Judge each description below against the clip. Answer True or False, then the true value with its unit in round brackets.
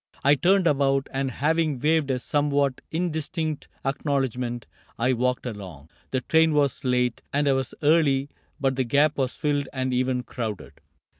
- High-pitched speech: False (135 Hz)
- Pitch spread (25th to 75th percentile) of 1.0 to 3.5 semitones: True (2.7 semitones)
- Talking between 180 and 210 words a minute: False (155 wpm)